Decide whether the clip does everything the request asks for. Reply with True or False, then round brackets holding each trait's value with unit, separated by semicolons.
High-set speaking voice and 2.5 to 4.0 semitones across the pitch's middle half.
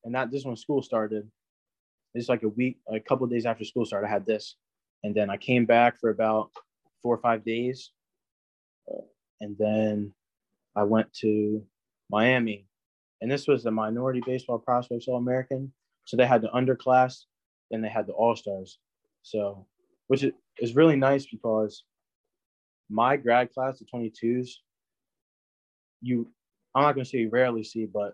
False (115 Hz; 3.0 semitones)